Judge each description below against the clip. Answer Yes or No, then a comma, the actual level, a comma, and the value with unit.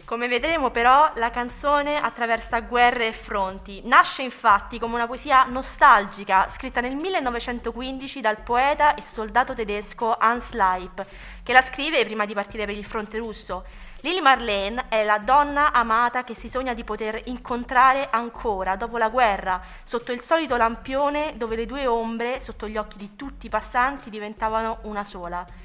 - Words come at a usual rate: Yes, average, 160 wpm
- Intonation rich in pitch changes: No, average, 3.3 semitones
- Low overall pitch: No, high, 235 Hz